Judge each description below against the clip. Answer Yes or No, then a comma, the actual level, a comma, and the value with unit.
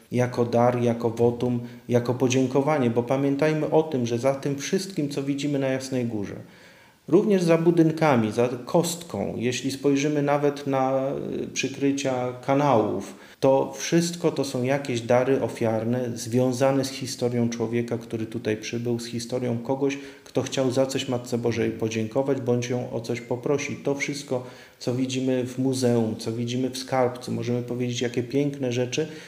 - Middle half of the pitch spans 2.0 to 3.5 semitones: Yes, narrow, 2.5 semitones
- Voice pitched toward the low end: Yes, low, 125 Hz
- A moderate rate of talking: Yes, average, 150 wpm